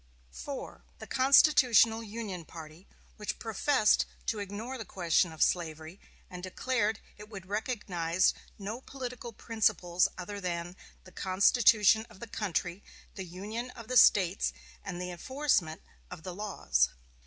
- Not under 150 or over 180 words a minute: No, slow, 135 wpm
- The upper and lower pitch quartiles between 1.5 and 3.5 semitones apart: No, average, 4.3 semitones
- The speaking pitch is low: No, high, 200 Hz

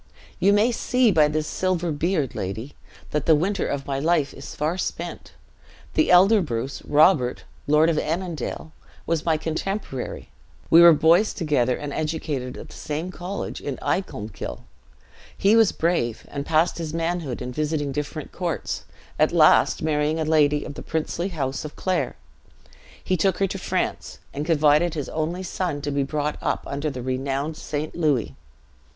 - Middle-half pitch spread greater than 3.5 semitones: No, average, 3.2 semitones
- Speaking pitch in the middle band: Yes, medium, 155 Hz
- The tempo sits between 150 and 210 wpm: Yes, average, 165 wpm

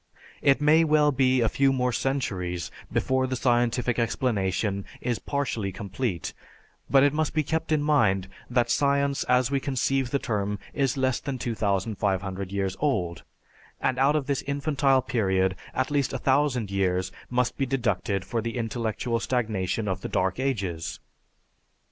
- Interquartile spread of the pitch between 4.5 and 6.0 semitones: Yes, wide, 5.4 semitones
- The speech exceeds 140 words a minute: Yes, average, 155 wpm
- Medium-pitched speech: No, low, 125 Hz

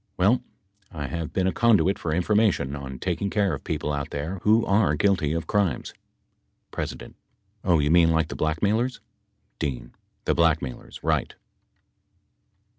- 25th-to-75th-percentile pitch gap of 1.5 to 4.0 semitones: No, average, 5.0 semitones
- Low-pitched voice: Yes, very low, 85 Hz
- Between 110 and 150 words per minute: Yes, average, 145 wpm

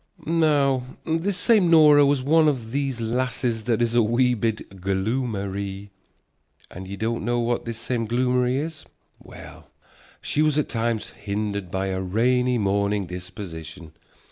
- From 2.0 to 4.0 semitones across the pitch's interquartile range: No, average, 4.9 semitones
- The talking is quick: No, average, 145 wpm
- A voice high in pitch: No, low, 115 Hz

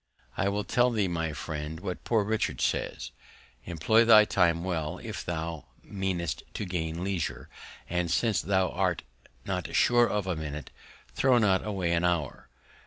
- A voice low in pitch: Yes, very low, 90 Hz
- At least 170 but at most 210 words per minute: No, average, 160 wpm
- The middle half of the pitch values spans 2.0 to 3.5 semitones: No, average, 4.0 semitones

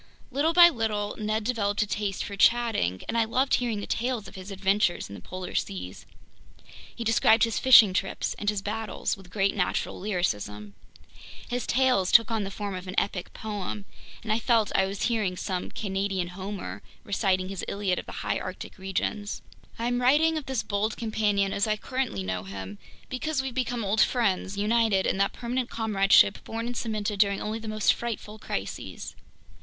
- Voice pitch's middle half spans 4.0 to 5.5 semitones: No, average, 3.1 semitones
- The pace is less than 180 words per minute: No, average, 185 wpm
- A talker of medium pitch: No, high, 210 Hz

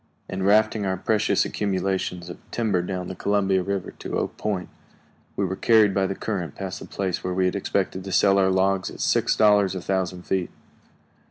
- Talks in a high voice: No, very low, 95 Hz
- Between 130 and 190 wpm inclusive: No, average, 200 wpm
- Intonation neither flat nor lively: No, narrow, 1.4 semitones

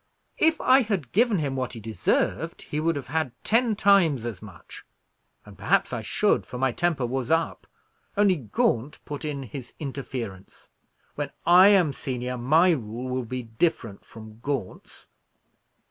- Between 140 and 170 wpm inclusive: Yes, average, 160 wpm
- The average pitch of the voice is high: No, low, 135 Hz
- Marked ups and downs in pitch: Yes, wide, 6.1 semitones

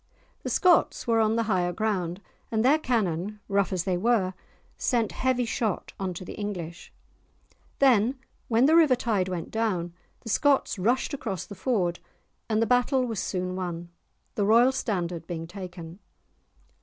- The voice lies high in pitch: Yes, high, 210 Hz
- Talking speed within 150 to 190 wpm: Yes, average, 160 wpm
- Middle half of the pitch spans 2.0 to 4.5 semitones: No, average, 5.0 semitones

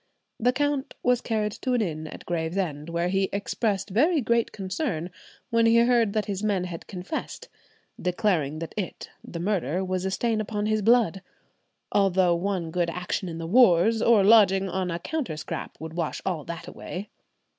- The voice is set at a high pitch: Yes, high, 195 Hz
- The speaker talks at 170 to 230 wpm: Yes, average, 175 wpm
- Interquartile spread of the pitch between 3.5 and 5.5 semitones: Yes, average, 4.5 semitones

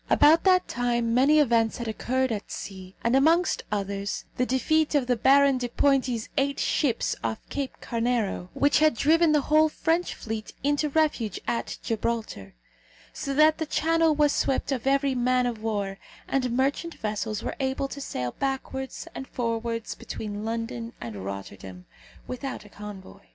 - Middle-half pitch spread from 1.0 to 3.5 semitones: No, average, 4.3 semitones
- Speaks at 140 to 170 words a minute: Yes, average, 160 wpm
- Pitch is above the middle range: Yes, very high, 250 Hz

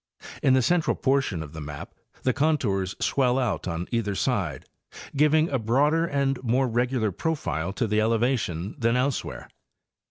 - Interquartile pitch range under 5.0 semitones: No, average, 5.3 semitones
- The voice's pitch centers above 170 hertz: No, low, 120 Hz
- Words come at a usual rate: Yes, average, 160 wpm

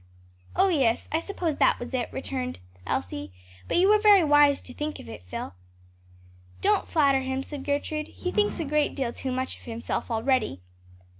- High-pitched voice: Yes, very high, 275 Hz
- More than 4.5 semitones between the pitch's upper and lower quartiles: No, average, 4.0 semitones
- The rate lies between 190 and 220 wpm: No, average, 180 wpm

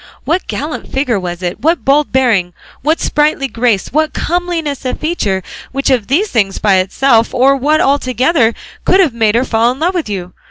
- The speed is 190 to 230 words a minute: Yes, average, 195 wpm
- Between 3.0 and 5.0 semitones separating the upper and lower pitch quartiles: No, wide, 5.5 semitones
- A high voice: Yes, very high, 265 Hz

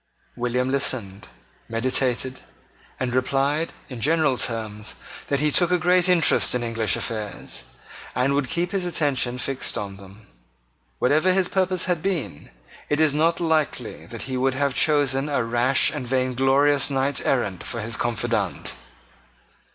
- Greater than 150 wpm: No, average, 145 wpm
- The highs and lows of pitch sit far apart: No, average, 4.2 semitones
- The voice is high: No, low, 135 Hz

